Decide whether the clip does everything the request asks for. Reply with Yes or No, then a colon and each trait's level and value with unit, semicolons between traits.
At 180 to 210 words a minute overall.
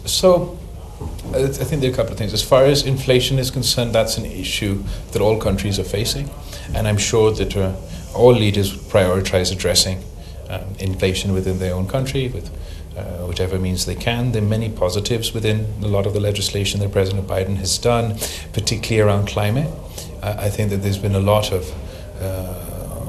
Yes: average, 185 wpm